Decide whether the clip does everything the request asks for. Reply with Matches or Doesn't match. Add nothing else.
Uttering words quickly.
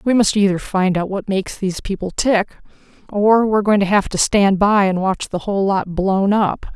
Matches